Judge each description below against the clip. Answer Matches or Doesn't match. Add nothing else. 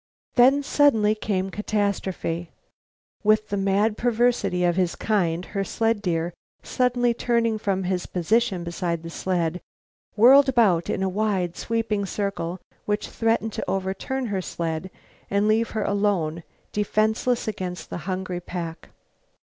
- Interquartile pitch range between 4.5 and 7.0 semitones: Doesn't match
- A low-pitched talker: Doesn't match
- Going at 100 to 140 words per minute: Matches